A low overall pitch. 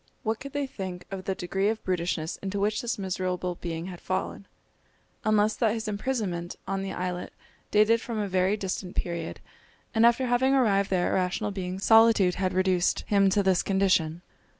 No: high, 195 Hz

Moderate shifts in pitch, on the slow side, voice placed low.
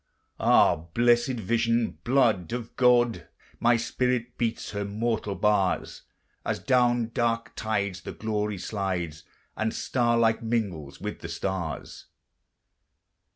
Yes: average, 3.0 semitones; slow, 115 wpm; low, 115 Hz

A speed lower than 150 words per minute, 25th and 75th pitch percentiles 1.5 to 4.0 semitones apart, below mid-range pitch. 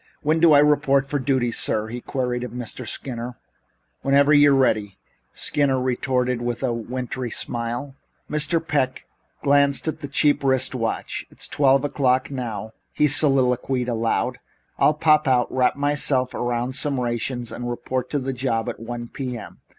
No: average, 160 wpm; average, 2.7 semitones; low, 130 Hz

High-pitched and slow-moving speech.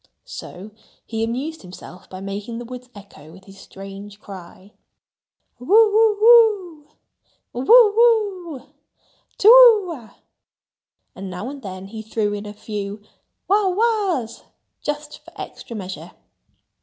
Yes: high, 240 Hz; slow, 130 wpm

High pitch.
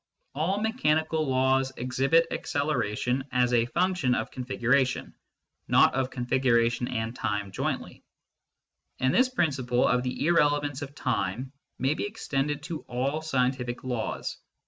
No: low, 130 Hz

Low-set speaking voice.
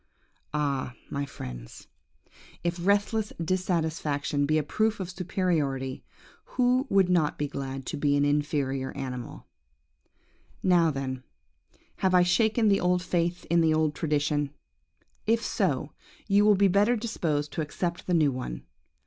No: medium, 160 Hz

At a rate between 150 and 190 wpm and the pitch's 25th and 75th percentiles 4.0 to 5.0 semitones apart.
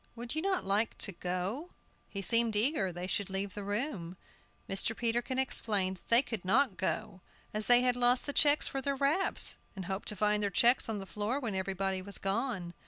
No: fast, 205 wpm; average, 4.4 semitones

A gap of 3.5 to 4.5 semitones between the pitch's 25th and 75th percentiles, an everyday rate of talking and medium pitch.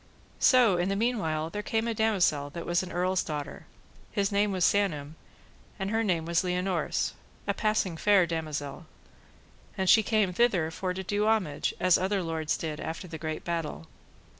Yes: average, 4.2 semitones; average, 180 wpm; medium, 180 Hz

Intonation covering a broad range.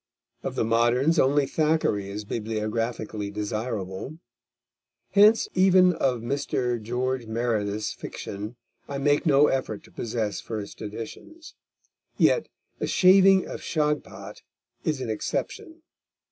Yes: wide, 5.8 semitones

